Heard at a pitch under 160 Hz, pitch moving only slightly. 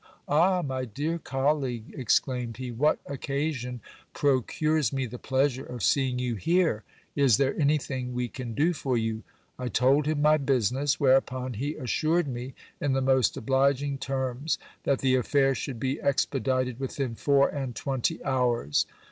Yes: low, 135 Hz; narrow, 2.3 semitones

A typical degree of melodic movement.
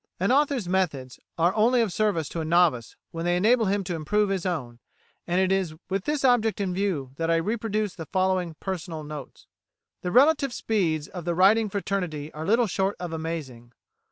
Yes: average, 4.4 semitones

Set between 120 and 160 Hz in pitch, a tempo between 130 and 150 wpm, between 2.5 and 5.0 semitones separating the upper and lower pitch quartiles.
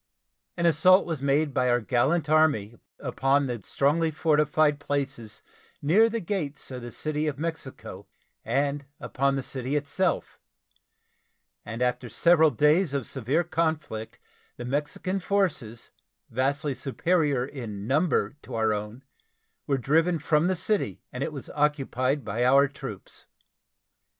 Yes: medium, 140 Hz; slow, 135 wpm; average, 3.8 semitones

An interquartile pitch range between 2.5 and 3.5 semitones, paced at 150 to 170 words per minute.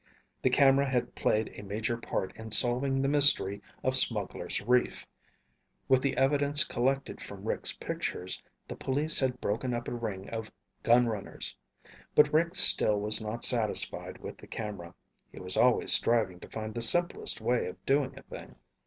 No: average, 4.0 semitones; average, 165 wpm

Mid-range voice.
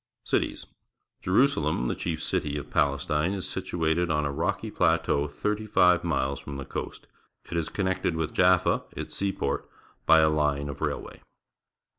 No: very low, 80 Hz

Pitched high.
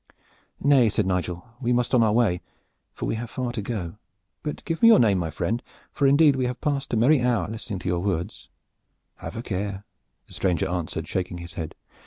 No: low, 110 Hz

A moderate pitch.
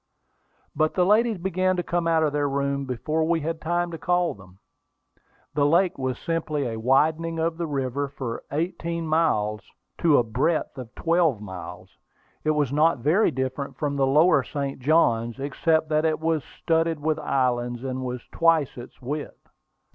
Yes: medium, 150 Hz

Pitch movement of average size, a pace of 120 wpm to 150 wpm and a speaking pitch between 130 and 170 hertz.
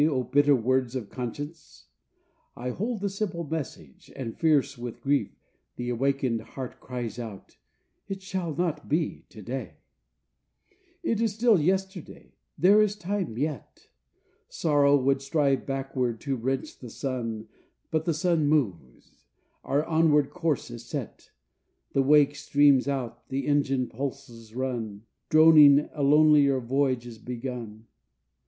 Yes: average, 4.2 semitones; slow, 135 wpm; medium, 140 Hz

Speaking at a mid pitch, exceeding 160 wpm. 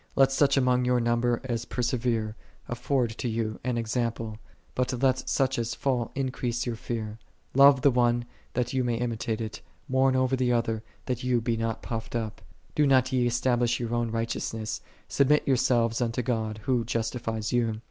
No: low, 120 Hz; average, 175 wpm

